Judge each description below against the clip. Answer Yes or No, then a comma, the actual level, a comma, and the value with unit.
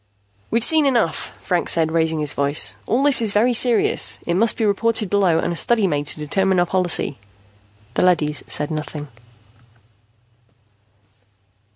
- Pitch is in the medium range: Yes, medium, 180 Hz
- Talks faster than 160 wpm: No, average, 155 wpm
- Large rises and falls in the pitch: Yes, wide, 6.2 semitones